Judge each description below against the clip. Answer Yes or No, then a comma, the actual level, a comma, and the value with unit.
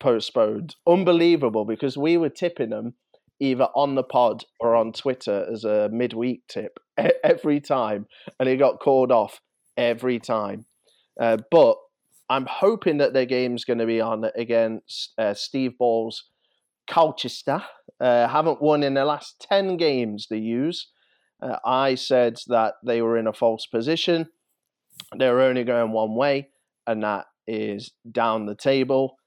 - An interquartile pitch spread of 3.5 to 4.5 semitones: Yes, average, 4.1 semitones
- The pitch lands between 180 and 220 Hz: No, low, 125 Hz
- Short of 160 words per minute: Yes, average, 150 wpm